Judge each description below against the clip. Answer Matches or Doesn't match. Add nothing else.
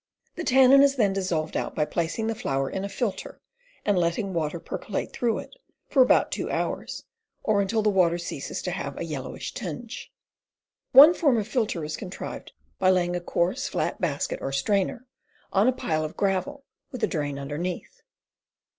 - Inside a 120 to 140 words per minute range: Doesn't match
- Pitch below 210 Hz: Matches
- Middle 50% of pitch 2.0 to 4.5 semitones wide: Doesn't match